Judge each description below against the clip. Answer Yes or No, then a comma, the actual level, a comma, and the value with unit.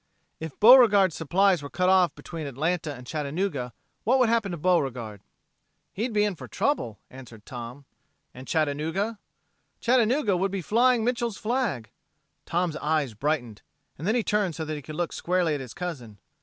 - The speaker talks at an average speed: Yes, average, 165 wpm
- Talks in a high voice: No, medium, 170 Hz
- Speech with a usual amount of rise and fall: No, wide, 6.7 semitones